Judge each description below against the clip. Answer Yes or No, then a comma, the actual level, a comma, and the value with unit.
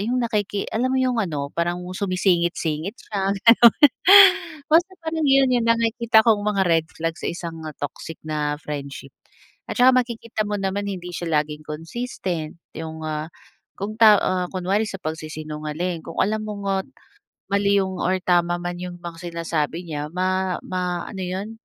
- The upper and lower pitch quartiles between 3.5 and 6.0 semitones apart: Yes, average, 4.4 semitones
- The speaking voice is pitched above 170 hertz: Yes, medium, 185 Hz